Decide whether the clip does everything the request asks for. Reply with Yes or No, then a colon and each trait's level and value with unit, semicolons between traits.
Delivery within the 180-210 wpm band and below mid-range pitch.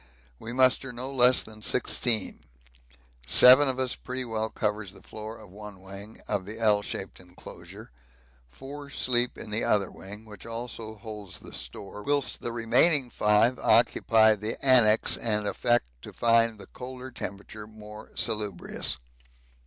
No: average, 150 wpm; low, 110 Hz